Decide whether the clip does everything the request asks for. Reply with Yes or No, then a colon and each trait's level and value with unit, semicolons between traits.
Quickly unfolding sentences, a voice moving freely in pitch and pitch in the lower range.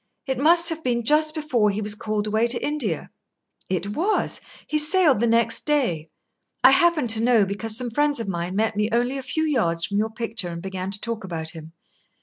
No: fast, 210 wpm; wide, 6.5 semitones; high, 230 Hz